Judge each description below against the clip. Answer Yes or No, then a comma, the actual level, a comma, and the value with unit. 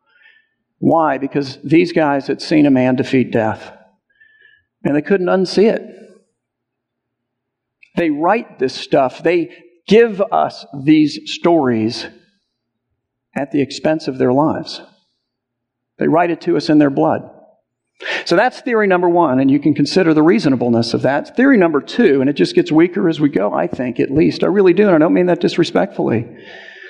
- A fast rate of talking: No, average, 170 wpm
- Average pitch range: No, wide, 6.2 semitones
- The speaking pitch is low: No, medium, 155 Hz